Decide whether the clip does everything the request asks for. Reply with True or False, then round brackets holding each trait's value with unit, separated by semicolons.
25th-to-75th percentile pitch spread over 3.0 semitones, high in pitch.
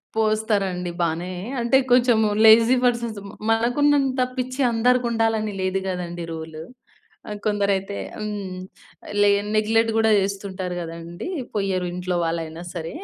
True (4.0 semitones; 205 Hz)